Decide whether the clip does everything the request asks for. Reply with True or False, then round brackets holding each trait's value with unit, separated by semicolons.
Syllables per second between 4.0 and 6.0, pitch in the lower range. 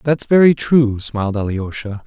True (4.6 syllables/s; 120 Hz)